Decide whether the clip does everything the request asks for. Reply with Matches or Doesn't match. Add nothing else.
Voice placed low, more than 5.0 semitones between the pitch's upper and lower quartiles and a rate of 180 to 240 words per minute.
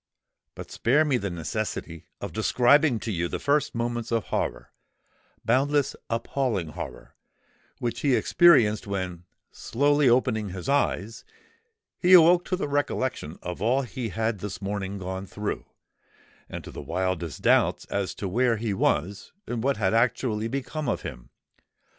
Doesn't match